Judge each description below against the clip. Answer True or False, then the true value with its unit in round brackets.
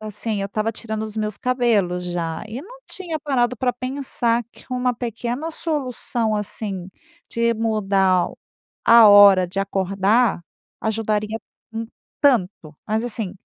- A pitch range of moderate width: True (3.5 semitones)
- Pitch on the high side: True (220 Hz)